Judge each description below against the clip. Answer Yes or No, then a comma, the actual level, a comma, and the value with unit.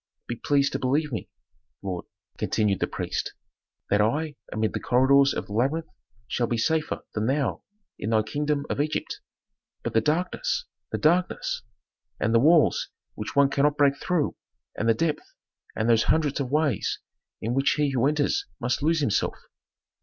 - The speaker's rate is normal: Yes, average, 170 wpm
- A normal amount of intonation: Yes, average, 4.8 semitones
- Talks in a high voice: No, medium, 140 Hz